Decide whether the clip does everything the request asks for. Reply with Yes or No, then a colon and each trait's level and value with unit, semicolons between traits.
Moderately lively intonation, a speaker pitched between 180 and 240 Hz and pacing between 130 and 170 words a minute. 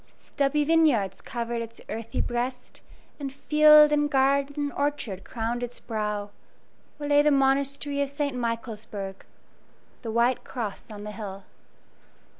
No: average, 4.3 semitones; very high, 250 Hz; slow, 135 wpm